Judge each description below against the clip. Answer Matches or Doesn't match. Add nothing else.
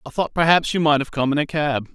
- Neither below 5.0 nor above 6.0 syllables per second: Doesn't match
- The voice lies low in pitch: Doesn't match